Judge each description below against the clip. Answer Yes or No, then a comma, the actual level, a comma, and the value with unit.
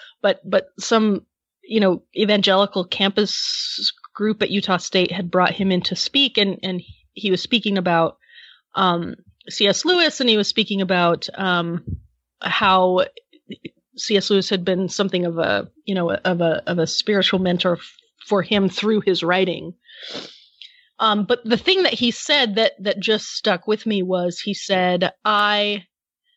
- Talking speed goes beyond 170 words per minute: No, average, 160 wpm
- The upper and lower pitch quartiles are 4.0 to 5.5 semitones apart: No, average, 3.3 semitones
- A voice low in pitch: No, high, 200 Hz